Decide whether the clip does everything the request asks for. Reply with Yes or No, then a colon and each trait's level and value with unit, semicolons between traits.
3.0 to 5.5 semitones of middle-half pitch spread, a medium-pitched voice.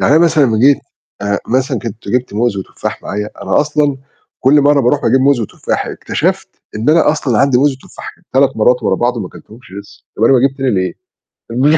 No: average, 4.2 semitones; low, 130 Hz